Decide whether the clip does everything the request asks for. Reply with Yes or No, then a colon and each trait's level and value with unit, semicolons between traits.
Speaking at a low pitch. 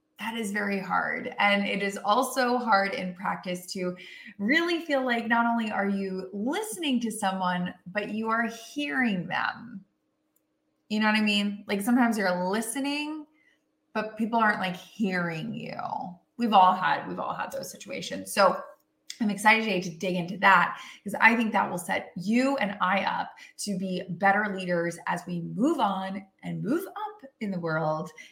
No: high, 210 Hz